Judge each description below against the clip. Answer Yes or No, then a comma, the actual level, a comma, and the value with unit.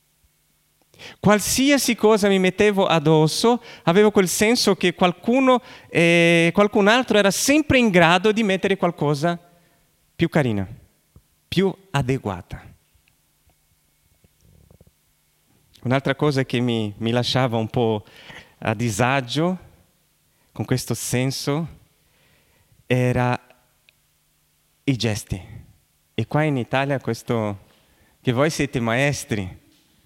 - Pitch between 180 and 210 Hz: No, low, 135 Hz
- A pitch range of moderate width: No, wide, 8.5 semitones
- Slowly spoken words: Yes, slow, 100 wpm